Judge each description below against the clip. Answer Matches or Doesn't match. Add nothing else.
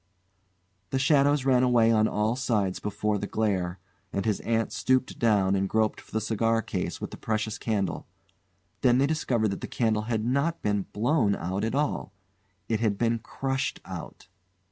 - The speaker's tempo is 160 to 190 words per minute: Matches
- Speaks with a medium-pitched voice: Doesn't match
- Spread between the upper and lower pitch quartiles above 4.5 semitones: Doesn't match